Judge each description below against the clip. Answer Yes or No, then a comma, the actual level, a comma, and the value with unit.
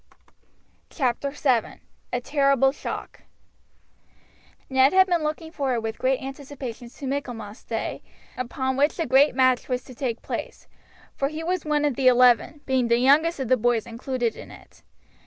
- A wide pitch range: No, average, 2.7 semitones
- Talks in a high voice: Yes, very high, 265 Hz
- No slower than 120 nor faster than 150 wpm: No, average, 160 wpm